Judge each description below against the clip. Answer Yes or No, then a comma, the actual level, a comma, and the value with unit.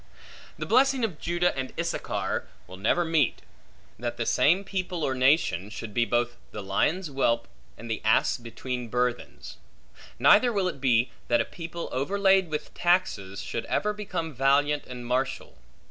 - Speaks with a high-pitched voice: No, low, 135 Hz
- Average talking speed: Yes, average, 160 wpm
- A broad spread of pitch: Yes, wide, 6.8 semitones